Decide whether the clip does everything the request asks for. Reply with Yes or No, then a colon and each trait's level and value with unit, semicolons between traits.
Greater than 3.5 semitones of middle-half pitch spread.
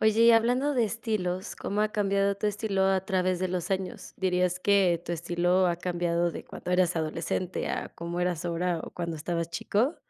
No: average, 2.7 semitones